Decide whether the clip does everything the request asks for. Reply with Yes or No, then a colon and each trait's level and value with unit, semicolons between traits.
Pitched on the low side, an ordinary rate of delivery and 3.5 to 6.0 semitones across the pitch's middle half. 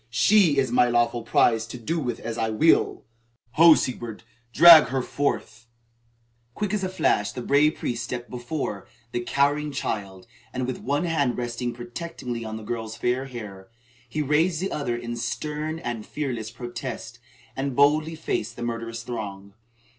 Yes: low, 120 Hz; average, 165 wpm; average, 4.3 semitones